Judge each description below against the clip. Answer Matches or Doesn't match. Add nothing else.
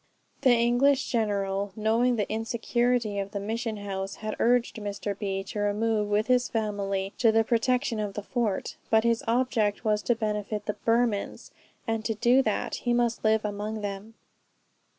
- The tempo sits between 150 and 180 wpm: Matches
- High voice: Matches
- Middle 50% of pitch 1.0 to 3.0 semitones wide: Matches